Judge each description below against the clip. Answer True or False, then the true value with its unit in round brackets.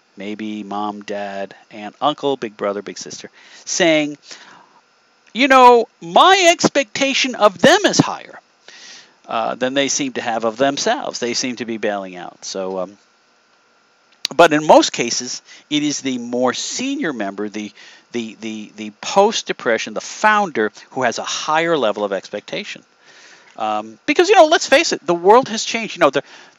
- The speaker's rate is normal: True (160 wpm)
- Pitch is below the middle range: True (125 Hz)